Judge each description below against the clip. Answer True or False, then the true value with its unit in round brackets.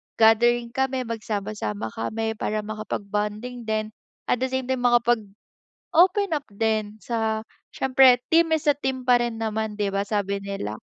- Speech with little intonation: False (3.3 semitones)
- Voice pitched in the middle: False (225 Hz)